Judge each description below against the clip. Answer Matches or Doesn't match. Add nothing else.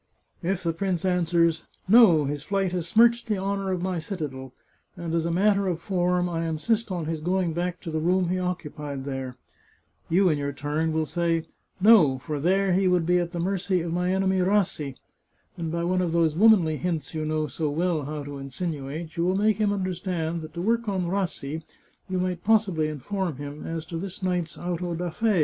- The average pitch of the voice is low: Doesn't match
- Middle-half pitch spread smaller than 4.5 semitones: Matches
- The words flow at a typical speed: Doesn't match